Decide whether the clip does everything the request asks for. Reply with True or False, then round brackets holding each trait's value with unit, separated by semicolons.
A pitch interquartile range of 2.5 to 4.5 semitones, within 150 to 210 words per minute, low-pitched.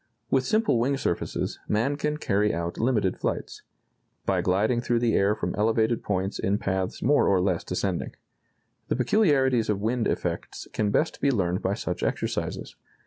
False (5.0 semitones; 165 wpm; 110 Hz)